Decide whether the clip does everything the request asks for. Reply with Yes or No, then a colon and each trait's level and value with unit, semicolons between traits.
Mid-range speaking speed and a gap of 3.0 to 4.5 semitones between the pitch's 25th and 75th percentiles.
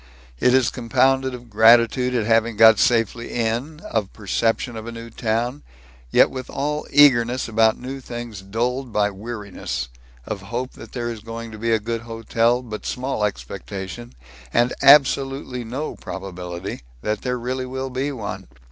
No: average, 160 wpm; narrow, 2.6 semitones